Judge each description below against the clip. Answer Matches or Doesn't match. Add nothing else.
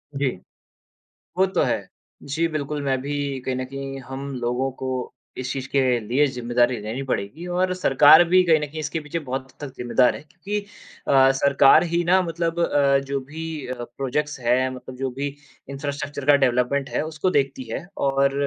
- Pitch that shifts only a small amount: Doesn't match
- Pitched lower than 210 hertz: Matches